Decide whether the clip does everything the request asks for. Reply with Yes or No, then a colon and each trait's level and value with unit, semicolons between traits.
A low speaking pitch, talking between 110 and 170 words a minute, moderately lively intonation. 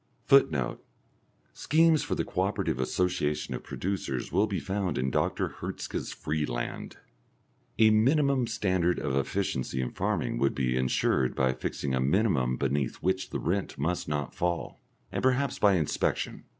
No: very low, 85 Hz; average, 150 wpm; wide, 7.3 semitones